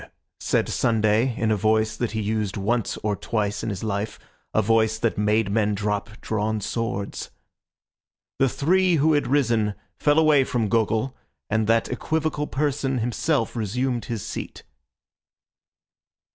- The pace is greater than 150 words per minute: No, average, 145 wpm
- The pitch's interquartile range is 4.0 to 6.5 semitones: No, average, 3.5 semitones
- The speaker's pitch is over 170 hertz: No, low, 110 Hz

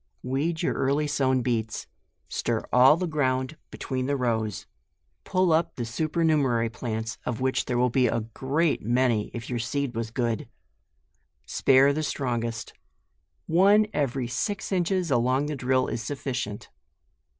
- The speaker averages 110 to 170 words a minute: Yes, average, 150 wpm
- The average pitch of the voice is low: Yes, low, 130 Hz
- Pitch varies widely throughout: No, average, 4.1 semitones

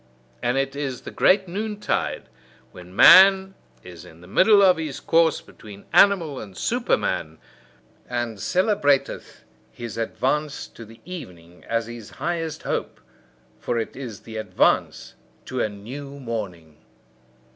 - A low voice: Yes, low, 130 Hz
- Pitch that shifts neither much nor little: No, wide, 7.7 semitones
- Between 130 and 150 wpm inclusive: Yes, slow, 135 wpm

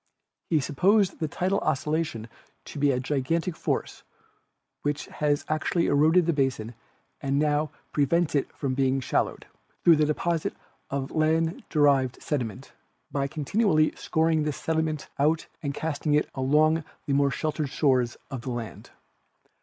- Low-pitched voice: No, medium, 150 Hz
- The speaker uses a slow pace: No, average, 150 wpm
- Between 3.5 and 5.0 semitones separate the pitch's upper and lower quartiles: No, narrow, 2.6 semitones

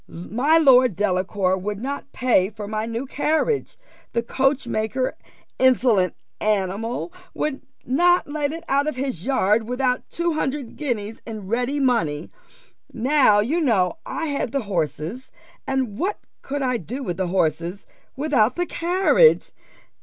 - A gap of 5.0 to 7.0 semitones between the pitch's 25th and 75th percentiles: Yes, wide, 5.5 semitones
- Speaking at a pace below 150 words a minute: Yes, average, 140 wpm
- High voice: Yes, very high, 250 Hz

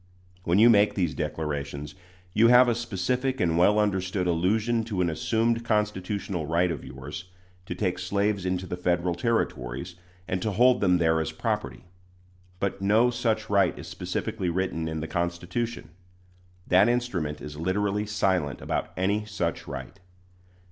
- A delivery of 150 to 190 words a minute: Yes, average, 155 wpm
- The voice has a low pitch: Yes, very low, 95 Hz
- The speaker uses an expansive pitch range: No, average, 3.8 semitones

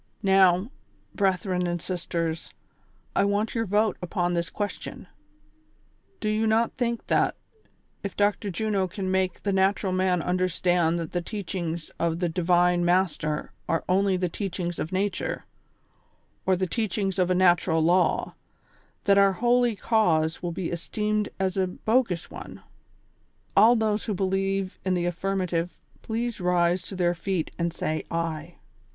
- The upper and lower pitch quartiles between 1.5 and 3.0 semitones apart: Yes, narrow, 2.5 semitones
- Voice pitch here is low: No, medium, 185 Hz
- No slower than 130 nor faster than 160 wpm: Yes, average, 145 wpm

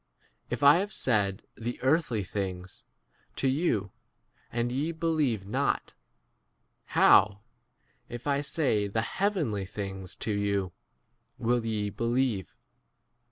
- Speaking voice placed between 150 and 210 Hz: No, low, 115 Hz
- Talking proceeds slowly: Yes, slow, 115 wpm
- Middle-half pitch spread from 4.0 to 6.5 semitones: Yes, wide, 5.6 semitones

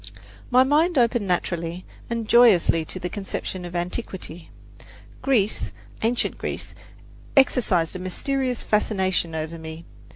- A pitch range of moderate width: No, wide, 5.7 semitones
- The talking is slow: Yes, slow, 120 wpm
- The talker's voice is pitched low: No, high, 190 Hz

